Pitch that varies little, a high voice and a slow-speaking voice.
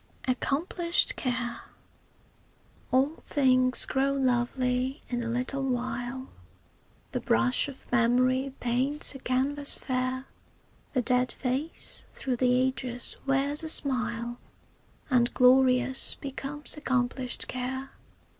Yes: narrow, 1.5 semitones; very high, 255 Hz; slow, 105 wpm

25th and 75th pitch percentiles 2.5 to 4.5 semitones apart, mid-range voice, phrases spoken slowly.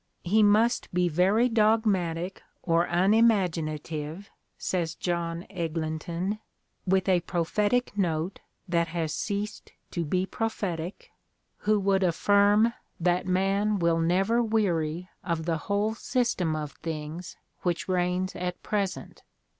Yes: average, 3.4 semitones; medium, 180 Hz; slow, 115 wpm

